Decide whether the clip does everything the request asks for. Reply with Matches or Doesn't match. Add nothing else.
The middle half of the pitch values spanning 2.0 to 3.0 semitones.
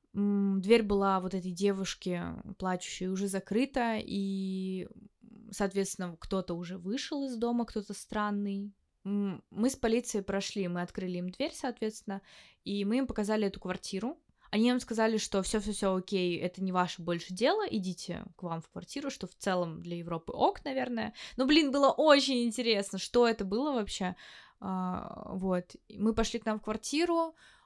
Doesn't match